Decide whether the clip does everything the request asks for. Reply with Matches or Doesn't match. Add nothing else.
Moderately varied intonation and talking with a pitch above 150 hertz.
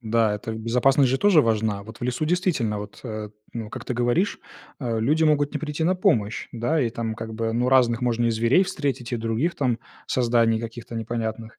Doesn't match